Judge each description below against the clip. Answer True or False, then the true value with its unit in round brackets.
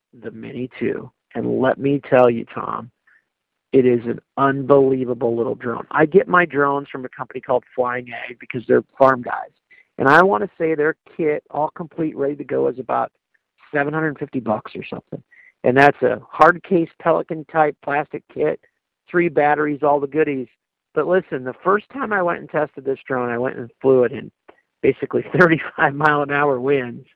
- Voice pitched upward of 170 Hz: False (140 Hz)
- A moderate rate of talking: True (195 wpm)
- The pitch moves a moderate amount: True (3.6 semitones)